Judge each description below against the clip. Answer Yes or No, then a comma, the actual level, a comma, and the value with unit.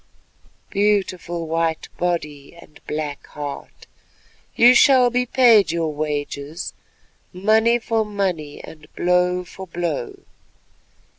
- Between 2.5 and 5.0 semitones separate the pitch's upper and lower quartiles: No, wide, 5.5 semitones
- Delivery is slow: Yes, slow, 100 wpm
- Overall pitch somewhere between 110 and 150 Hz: No, medium, 175 Hz